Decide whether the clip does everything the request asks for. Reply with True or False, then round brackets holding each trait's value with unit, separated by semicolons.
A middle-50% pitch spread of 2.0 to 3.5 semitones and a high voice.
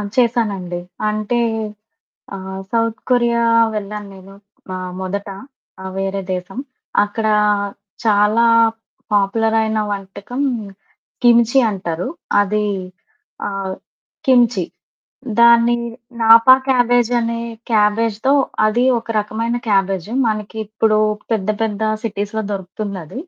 True (2.8 semitones; 215 Hz)